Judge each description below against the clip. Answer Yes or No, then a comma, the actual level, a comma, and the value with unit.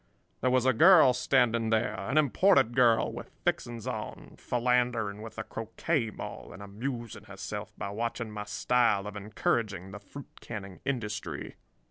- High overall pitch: No, low, 115 Hz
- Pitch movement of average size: Yes, average, 3.2 semitones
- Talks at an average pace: Yes, average, 145 wpm